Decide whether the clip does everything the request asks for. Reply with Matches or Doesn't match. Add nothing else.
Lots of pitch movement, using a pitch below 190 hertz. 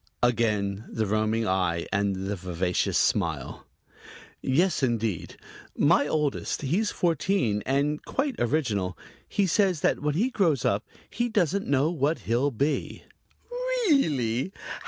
Matches